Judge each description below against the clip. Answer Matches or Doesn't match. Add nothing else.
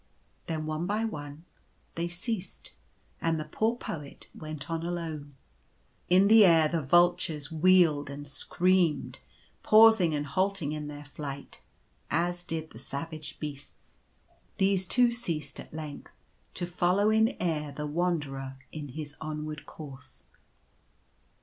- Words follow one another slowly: Matches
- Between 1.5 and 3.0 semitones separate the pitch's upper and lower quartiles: Doesn't match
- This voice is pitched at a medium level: Matches